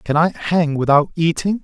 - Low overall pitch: No, medium, 160 Hz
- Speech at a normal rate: Yes, average, 185 wpm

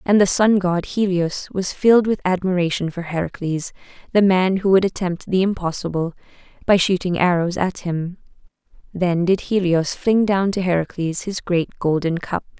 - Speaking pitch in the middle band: Yes, medium, 180 Hz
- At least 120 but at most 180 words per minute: Yes, average, 160 wpm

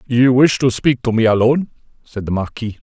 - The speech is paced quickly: Yes, fast, 210 wpm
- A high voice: No, low, 120 Hz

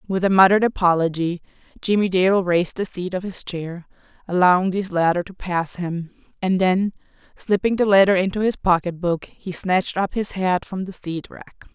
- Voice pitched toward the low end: No, medium, 185 Hz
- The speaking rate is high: No, average, 175 wpm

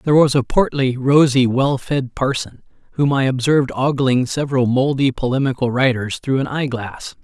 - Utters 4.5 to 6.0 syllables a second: Yes, 5.1 syllables/s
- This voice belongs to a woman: No, male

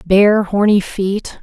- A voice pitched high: Yes, high, 200 Hz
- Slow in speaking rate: Yes, slow, 125 wpm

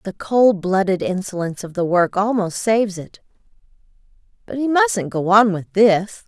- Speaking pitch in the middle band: No, high, 195 Hz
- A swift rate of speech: No, average, 165 wpm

